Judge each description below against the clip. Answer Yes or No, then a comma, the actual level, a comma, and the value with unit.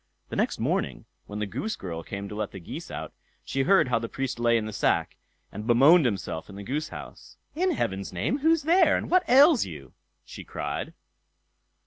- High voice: No, low, 120 Hz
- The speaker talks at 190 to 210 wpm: Yes, average, 200 wpm